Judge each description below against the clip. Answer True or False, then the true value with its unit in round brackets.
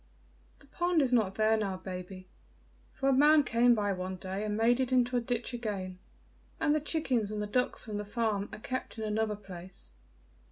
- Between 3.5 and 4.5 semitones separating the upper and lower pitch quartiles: True (3.9 semitones)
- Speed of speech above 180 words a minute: True (200 wpm)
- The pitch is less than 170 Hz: False (220 Hz)